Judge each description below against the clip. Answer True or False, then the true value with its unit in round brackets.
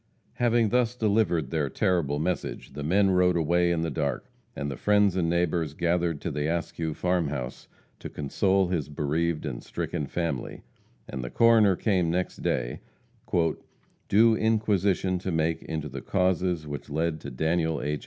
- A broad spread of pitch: False (3.8 semitones)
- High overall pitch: False (85 Hz)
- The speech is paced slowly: False (165 wpm)